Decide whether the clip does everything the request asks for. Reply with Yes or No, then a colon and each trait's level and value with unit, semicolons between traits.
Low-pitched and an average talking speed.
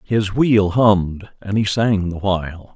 Yes: low, 100 Hz; average, 175 wpm